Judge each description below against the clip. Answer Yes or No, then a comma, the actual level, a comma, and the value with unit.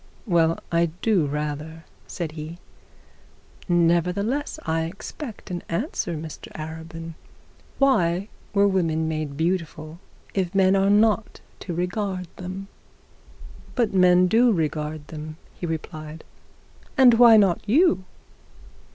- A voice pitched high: No, medium, 175 Hz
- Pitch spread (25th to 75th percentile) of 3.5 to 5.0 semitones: Yes, average, 3.8 semitones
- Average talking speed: No, slow, 115 wpm